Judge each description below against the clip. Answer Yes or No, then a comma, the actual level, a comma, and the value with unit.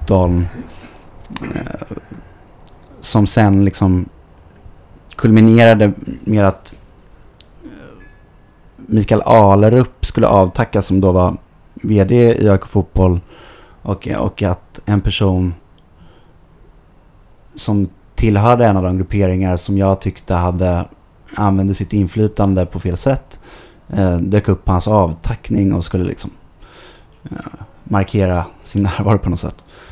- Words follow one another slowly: Yes, slow, 100 wpm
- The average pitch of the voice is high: No, low, 100 Hz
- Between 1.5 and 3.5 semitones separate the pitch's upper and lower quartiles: Yes, average, 2.8 semitones